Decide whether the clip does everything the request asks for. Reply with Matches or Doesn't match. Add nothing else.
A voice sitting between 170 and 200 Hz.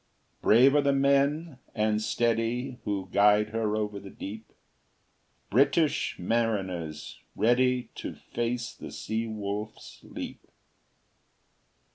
Doesn't match